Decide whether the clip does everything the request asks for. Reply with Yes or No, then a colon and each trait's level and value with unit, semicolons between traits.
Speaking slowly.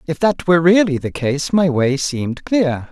No: fast, 205 wpm